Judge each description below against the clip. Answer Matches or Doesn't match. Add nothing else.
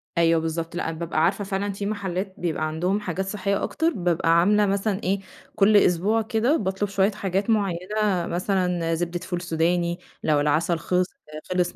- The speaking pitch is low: Doesn't match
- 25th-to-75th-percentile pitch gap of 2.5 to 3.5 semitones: Matches